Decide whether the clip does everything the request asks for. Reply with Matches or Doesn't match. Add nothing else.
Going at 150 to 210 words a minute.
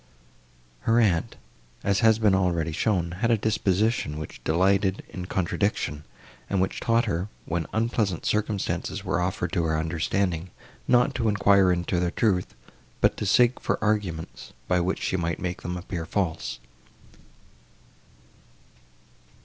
Doesn't match